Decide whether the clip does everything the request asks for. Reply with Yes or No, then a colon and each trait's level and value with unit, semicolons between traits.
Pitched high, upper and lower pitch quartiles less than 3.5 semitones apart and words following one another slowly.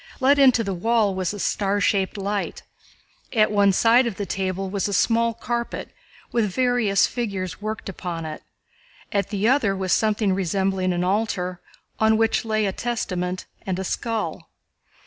No: high, 205 Hz; average, 3.1 semitones; average, 165 wpm